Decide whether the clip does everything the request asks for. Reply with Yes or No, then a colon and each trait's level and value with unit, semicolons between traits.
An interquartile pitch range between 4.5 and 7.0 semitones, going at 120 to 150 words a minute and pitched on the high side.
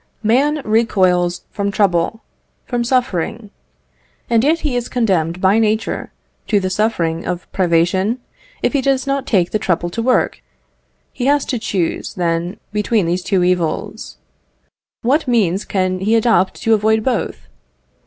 Yes: average, 4.8 semitones; average, 145 wpm; high, 210 Hz